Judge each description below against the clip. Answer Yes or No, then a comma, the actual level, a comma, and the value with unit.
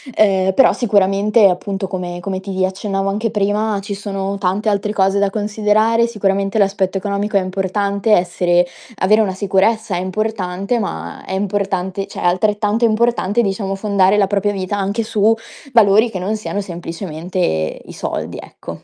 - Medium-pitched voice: No, high, 200 Hz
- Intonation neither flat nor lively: No, narrow, 1.9 semitones